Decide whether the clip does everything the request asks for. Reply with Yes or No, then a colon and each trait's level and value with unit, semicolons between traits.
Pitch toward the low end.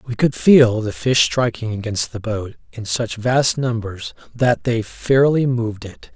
Yes: low, 115 Hz